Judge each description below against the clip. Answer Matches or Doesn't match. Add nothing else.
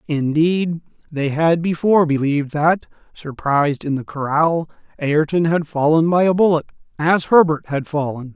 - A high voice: Doesn't match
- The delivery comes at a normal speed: Matches